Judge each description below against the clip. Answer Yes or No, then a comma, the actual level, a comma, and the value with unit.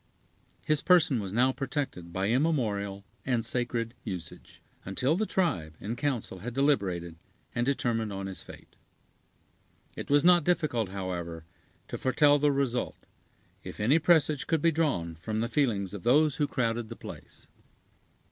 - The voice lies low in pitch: Yes, low, 120 Hz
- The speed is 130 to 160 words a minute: Yes, average, 150 wpm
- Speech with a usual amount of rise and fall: No, wide, 6.7 semitones